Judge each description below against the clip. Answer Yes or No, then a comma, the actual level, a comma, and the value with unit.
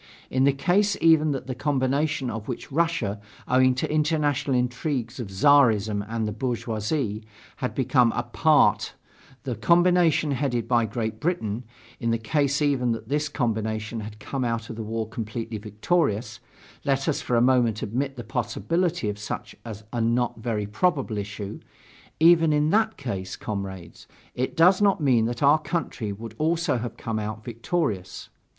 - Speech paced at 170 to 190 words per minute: No, average, 160 wpm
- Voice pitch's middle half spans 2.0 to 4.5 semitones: No, average, 5.1 semitones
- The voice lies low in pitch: Yes, low, 125 Hz